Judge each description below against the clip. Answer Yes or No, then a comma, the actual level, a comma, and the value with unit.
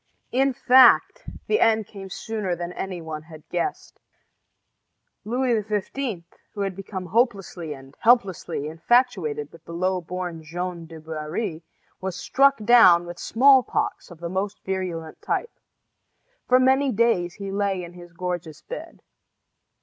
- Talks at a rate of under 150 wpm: Yes, average, 140 wpm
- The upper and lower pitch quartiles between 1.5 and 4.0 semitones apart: No, average, 5.2 semitones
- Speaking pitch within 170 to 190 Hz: Yes, medium, 185 Hz